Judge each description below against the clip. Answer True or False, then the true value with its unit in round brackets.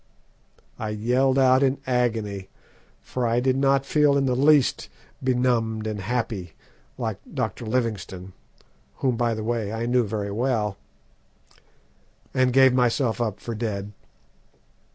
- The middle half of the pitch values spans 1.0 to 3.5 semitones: True (3.1 semitones)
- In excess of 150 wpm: False (135 wpm)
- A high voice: False (120 Hz)